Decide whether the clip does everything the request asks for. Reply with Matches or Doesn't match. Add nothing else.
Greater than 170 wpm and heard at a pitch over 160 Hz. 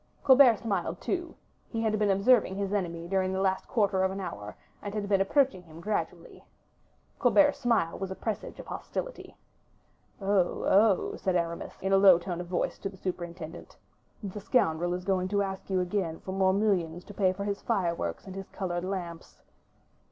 Matches